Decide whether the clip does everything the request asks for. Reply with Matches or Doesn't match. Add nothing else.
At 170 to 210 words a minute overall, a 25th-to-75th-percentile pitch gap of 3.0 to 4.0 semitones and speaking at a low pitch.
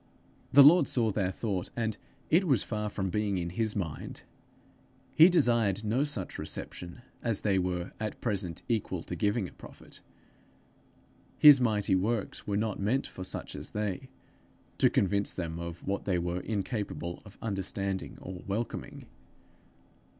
Doesn't match